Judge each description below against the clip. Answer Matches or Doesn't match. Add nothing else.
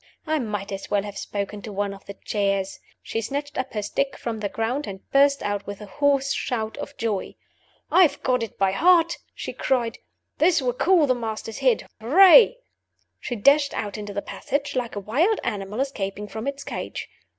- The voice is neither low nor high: Doesn't match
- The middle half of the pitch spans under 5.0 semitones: Doesn't match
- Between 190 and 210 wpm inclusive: Matches